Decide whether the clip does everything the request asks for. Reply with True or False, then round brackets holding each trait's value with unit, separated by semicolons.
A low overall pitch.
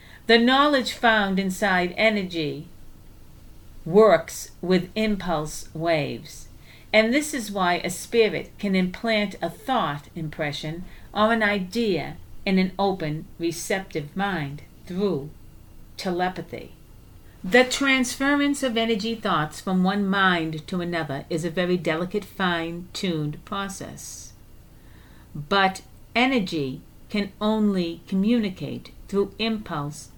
False (185 Hz)